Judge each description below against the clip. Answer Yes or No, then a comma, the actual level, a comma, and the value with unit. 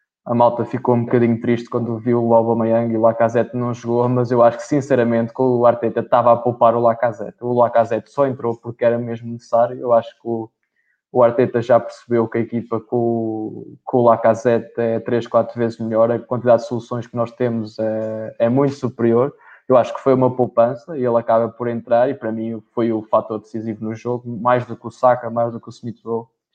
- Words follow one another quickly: Yes, fast, 220 wpm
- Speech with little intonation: Yes, narrow, 1.0 semitones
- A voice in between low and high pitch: No, low, 115 Hz